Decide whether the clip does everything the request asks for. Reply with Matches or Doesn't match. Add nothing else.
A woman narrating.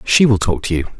Doesn't match